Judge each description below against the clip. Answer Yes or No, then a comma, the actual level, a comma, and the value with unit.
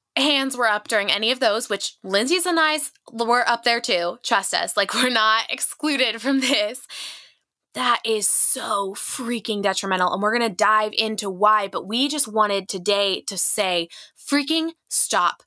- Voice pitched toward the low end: No, high, 220 Hz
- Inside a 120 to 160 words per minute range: No, average, 175 wpm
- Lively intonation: No, average, 4.0 semitones